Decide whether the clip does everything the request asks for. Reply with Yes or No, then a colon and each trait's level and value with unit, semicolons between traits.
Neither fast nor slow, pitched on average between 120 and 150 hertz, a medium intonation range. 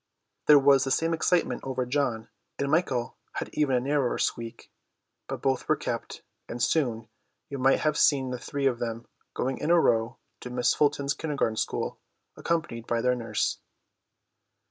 Yes: average, 165 wpm; low, 135 Hz; average, 3.4 semitones